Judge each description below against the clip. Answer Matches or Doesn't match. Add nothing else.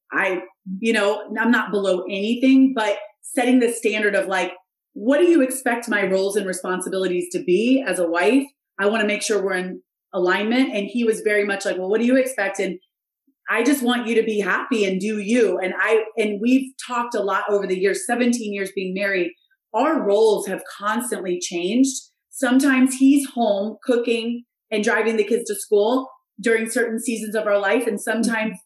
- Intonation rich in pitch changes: Doesn't match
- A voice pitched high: Matches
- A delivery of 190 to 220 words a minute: Matches